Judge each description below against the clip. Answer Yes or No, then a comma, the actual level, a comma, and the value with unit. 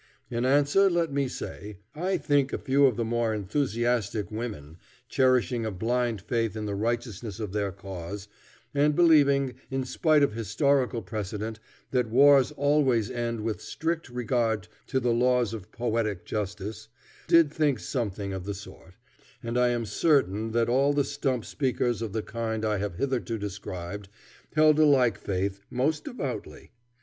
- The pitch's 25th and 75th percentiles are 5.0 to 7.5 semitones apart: No, average, 4.5 semitones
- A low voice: Yes, low, 120 Hz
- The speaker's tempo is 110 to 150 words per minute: No, average, 160 wpm